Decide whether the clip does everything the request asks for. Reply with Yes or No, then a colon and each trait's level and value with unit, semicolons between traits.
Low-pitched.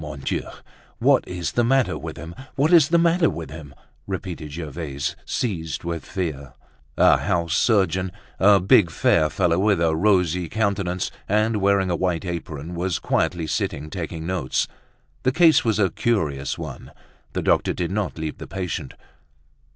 Yes: very low, 90 Hz